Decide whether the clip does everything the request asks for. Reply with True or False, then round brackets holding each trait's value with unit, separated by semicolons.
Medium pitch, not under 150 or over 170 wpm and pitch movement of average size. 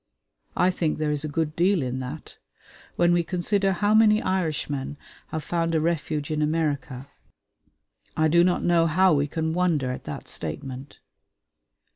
True (160 Hz; 160 wpm; 3.3 semitones)